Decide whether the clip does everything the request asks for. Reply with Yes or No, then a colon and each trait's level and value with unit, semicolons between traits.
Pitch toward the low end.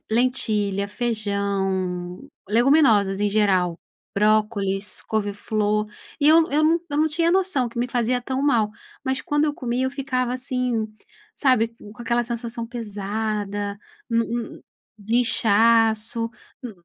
No: high, 230 Hz